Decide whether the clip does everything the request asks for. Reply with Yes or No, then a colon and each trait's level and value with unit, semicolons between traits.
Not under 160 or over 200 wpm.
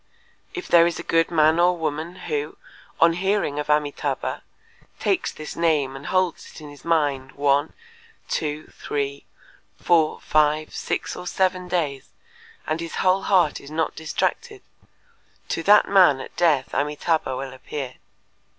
No: average, 150 wpm